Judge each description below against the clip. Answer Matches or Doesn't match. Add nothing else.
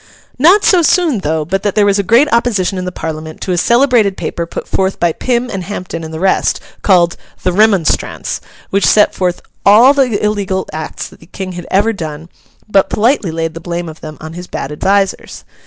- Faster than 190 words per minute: Matches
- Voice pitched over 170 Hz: Matches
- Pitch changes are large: Doesn't match